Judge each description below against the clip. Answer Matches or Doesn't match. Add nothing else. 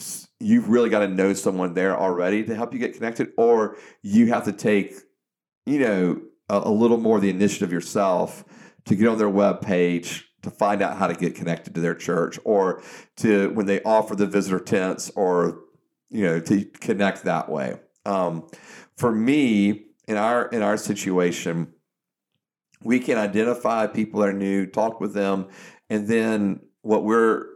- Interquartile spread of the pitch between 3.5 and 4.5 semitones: Doesn't match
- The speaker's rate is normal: Matches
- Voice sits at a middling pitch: Doesn't match